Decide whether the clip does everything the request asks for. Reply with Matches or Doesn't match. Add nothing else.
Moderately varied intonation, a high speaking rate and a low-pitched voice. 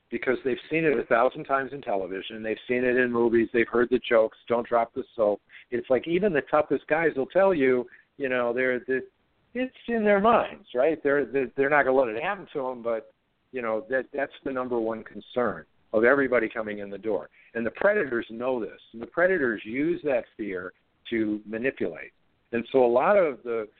Matches